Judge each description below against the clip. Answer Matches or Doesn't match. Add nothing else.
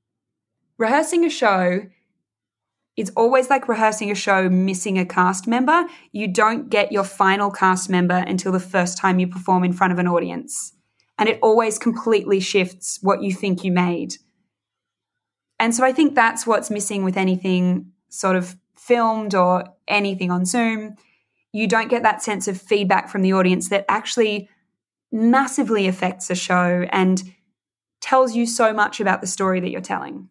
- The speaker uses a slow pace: Doesn't match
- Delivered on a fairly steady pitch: Doesn't match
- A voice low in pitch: Doesn't match